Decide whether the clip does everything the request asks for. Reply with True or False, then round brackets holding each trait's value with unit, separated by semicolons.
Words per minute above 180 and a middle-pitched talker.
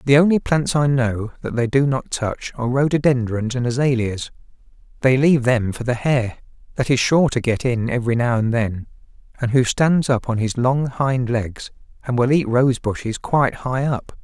False (200 wpm; 125 Hz)